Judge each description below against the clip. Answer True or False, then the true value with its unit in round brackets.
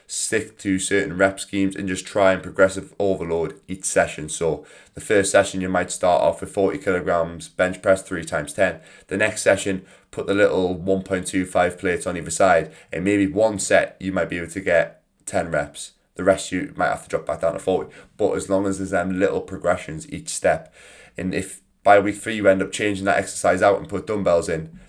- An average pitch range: False (1.2 semitones)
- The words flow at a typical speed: False (215 wpm)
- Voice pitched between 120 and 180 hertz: False (95 Hz)